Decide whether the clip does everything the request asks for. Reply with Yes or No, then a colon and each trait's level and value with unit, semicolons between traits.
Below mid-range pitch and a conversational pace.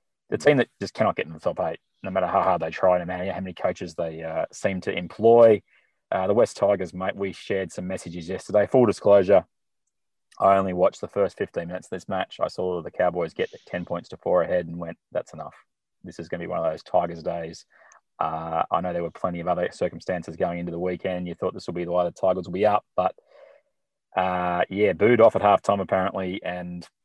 No: very low, 90 Hz; fast, 235 wpm